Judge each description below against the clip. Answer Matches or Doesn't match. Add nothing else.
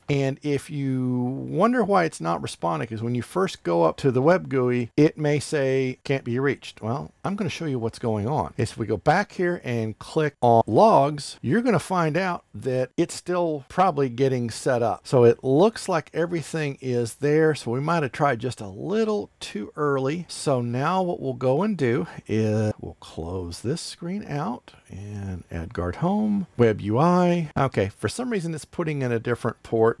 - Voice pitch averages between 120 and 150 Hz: Matches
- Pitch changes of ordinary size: Doesn't match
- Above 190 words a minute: Matches